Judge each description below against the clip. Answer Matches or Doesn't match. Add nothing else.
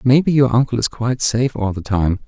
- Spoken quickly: Matches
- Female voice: Doesn't match